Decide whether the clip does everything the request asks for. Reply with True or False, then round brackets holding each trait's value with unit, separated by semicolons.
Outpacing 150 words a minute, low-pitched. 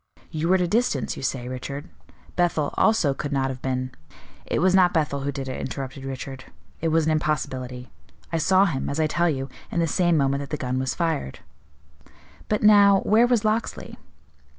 False (200 wpm; 150 Hz)